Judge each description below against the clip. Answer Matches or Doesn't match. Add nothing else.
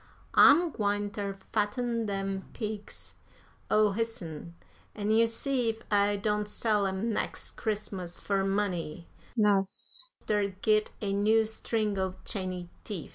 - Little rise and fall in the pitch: Matches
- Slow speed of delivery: Matches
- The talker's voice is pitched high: Matches